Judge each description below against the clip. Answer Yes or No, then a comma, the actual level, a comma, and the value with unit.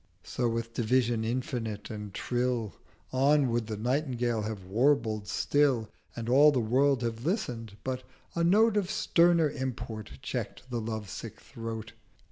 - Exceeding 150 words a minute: No, average, 145 wpm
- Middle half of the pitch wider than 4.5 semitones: No, average, 3.7 semitones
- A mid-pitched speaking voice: No, low, 120 Hz